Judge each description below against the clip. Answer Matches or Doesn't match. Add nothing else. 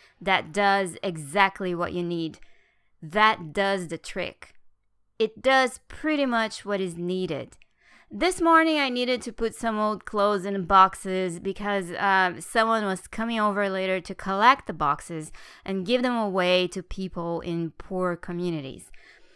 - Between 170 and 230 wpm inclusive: Doesn't match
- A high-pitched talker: Matches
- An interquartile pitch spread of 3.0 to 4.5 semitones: Matches